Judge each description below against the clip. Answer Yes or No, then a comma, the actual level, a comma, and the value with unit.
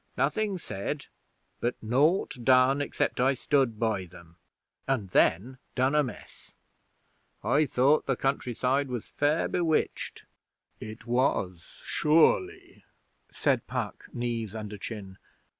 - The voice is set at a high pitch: No, low, 125 Hz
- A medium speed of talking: No, slow, 115 wpm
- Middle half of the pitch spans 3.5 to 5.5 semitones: Yes, average, 4.6 semitones